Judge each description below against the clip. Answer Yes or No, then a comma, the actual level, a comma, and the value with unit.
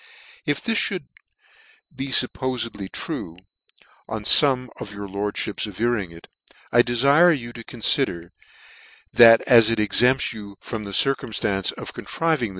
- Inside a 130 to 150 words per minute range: Yes, average, 140 wpm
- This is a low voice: Yes, low, 115 Hz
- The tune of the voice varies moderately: Yes, average, 4.2 semitones